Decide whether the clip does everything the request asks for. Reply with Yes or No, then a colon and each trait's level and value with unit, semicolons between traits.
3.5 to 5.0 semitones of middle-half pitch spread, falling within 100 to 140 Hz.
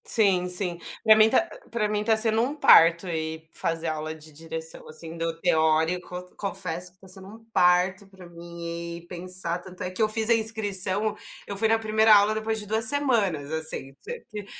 No: average, 4.4 semitones; medium, 185 Hz